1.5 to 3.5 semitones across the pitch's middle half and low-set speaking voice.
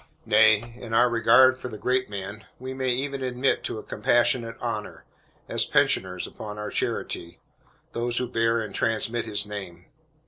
Yes: average, 2.8 semitones; low, 115 Hz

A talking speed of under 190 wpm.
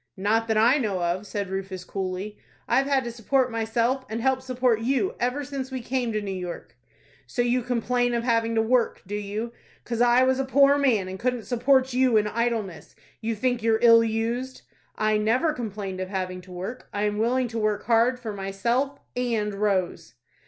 No: average, 195 wpm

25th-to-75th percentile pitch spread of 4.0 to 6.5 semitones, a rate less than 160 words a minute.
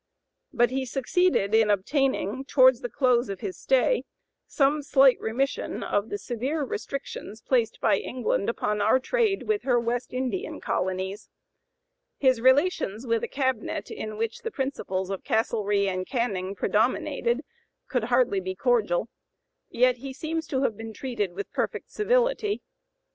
Yes: average, 4.6 semitones; average, 150 wpm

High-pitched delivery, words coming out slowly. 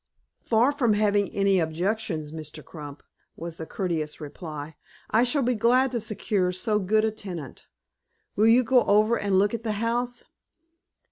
No: high, 205 Hz; average, 160 wpm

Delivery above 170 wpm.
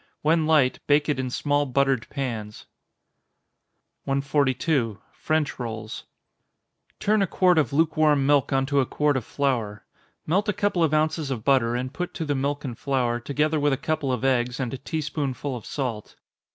Yes: average, 180 wpm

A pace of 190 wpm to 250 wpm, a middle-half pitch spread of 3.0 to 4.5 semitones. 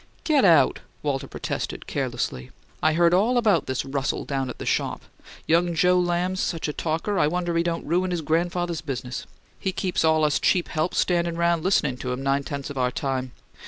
Yes: average, 195 wpm; average, 4.1 semitones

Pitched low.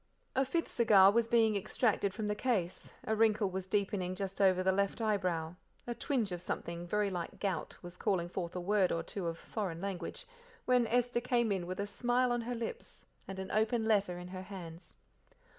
No: high, 200 Hz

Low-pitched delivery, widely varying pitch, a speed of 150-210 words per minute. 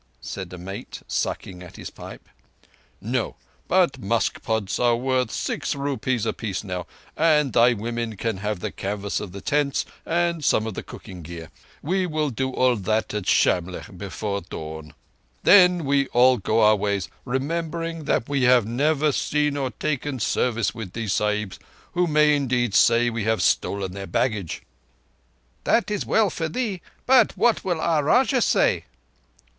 Yes: low, 120 Hz; wide, 6.7 semitones; average, 165 wpm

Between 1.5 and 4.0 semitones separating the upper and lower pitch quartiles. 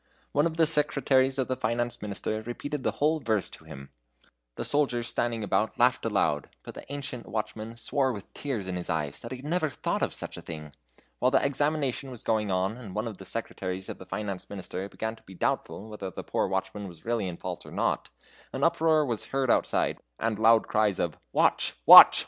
No: average, 5.1 semitones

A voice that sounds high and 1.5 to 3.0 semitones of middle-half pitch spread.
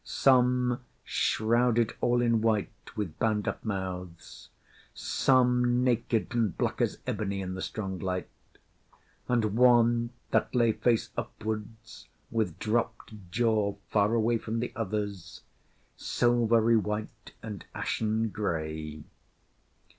No: low, 110 Hz; average, 2.7 semitones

